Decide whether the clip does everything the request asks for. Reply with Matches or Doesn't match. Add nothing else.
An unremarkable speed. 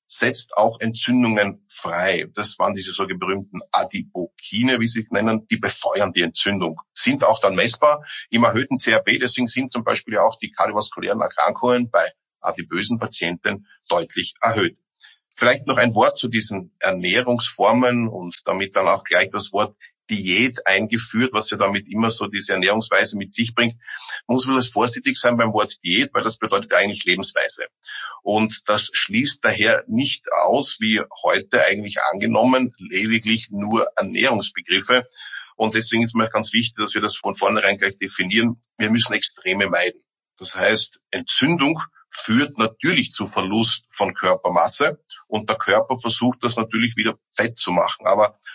Matches